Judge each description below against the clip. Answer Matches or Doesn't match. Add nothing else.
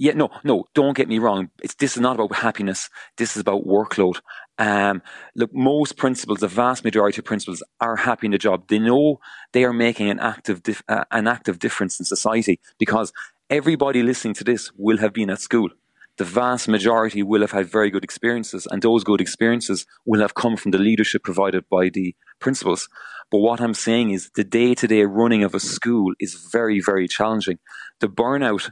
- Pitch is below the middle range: Matches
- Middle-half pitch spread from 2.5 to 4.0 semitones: Matches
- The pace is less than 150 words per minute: Doesn't match